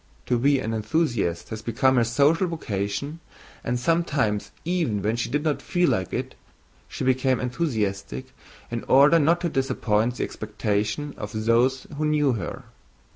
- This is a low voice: Yes, low, 125 Hz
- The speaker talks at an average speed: Yes, average, 155 wpm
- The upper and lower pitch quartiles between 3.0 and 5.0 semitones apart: No, wide, 5.5 semitones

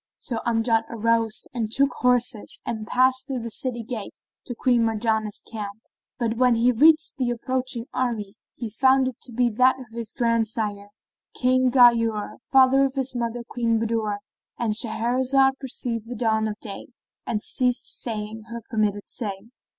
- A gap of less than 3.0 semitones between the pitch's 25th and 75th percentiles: Yes, narrow, 2.4 semitones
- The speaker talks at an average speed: Yes, average, 160 wpm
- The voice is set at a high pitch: Yes, high, 235 Hz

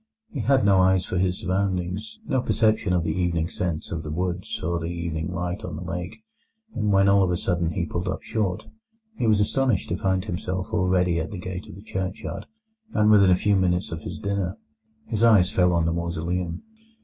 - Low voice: Yes, very low, 90 Hz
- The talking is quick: Yes, fast, 210 wpm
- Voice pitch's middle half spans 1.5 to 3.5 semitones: Yes, narrow, 2.4 semitones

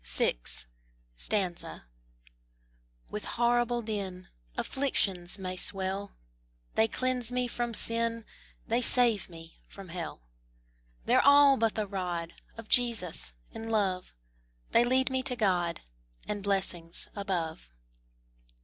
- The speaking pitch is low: No, high, 210 Hz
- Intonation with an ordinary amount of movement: Yes, average, 4.7 semitones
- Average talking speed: No, slow, 110 wpm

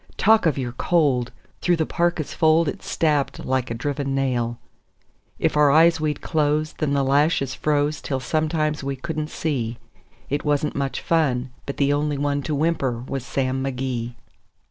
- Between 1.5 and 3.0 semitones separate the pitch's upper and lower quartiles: Yes, average, 2.7 semitones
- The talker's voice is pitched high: No, medium, 145 Hz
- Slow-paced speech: No, average, 165 wpm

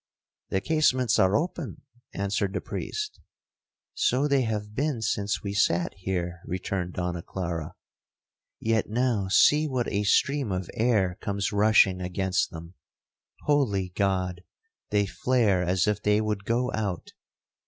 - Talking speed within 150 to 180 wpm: No, slow, 135 wpm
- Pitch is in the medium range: No, low, 100 Hz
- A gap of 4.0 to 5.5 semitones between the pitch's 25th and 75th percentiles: Yes, average, 4.3 semitones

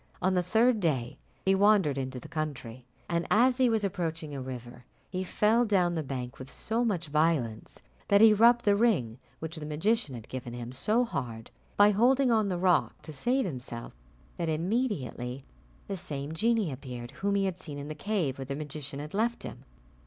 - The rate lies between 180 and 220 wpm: Yes, average, 195 wpm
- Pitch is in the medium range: Yes, medium, 165 Hz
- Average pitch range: No, wide, 7.7 semitones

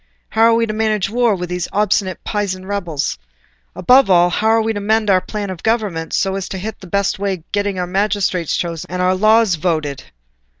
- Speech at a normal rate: No, fast, 225 wpm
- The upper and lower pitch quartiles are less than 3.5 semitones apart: Yes, average, 3.1 semitones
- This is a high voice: Yes, high, 195 Hz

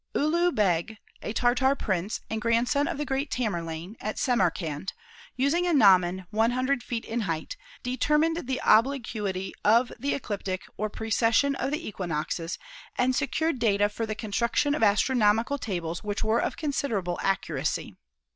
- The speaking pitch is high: Yes, high, 225 Hz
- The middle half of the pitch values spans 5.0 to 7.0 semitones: Yes, average, 5.3 semitones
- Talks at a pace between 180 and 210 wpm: No, average, 145 wpm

